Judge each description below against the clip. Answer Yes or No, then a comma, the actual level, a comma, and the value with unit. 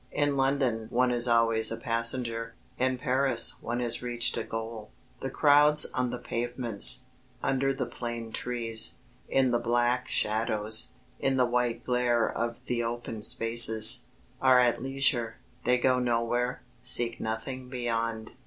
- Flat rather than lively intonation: Yes, narrow, 1.7 semitones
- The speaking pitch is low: Yes, low, 120 Hz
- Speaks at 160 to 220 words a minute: No, average, 145 wpm